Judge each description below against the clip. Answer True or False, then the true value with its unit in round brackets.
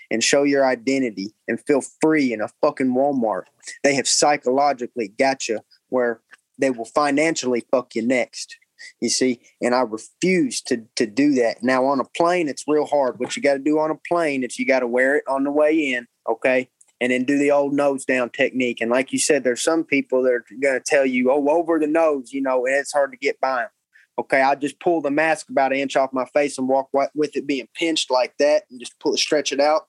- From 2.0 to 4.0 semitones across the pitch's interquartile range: True (2.9 semitones)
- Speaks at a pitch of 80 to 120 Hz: False (135 Hz)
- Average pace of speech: False (240 wpm)